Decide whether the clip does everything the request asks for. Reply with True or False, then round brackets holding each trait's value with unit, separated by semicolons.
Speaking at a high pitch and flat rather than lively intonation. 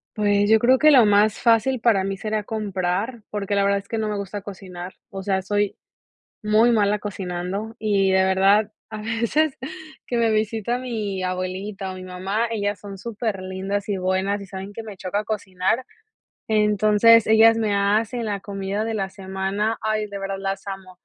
True (205 Hz; 2.2 semitones)